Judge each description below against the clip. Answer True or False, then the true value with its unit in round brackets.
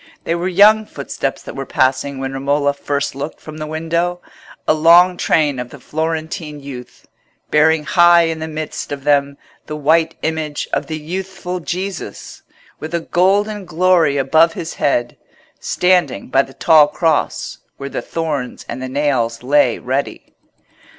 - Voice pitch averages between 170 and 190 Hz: False (155 Hz)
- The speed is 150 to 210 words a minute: True (155 wpm)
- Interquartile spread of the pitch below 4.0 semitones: True (3.3 semitones)